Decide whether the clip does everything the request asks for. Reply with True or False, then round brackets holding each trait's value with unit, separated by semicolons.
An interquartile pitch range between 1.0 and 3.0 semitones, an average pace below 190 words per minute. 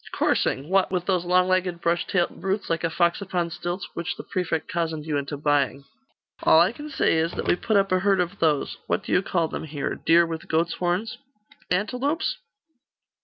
False (2.6 semitones; 205 wpm)